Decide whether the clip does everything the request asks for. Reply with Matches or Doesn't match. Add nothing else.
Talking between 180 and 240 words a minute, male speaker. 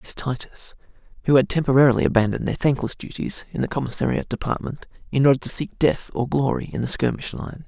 Matches